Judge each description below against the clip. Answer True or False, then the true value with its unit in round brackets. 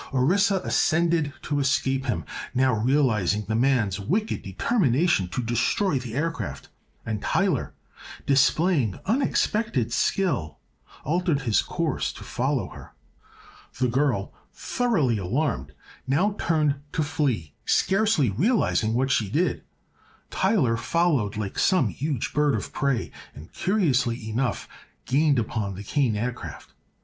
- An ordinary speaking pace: False (120 wpm)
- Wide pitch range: True (6.8 semitones)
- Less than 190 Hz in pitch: True (135 Hz)